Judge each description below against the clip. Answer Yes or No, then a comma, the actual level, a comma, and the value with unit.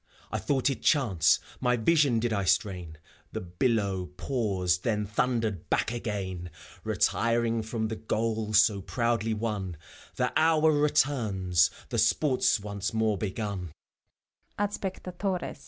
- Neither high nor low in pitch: No, low, 110 Hz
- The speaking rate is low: Yes, slow, 120 wpm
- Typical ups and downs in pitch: Yes, average, 3.6 semitones